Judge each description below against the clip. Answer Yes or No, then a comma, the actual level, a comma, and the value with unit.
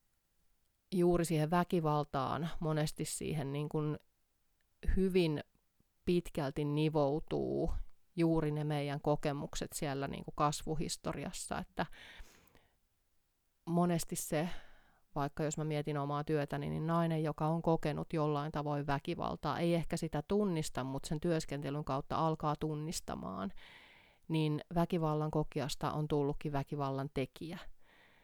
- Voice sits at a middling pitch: Yes, medium, 150 Hz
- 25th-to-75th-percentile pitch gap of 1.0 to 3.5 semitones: Yes, narrow, 2.4 semitones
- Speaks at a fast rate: No, average, 110 wpm